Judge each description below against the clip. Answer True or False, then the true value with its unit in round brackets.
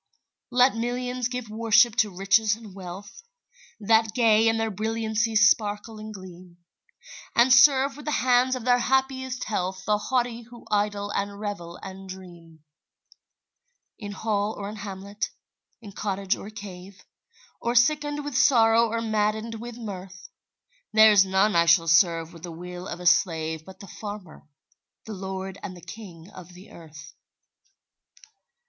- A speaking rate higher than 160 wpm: False (150 wpm)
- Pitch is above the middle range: True (210 Hz)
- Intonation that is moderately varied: True (3.5 semitones)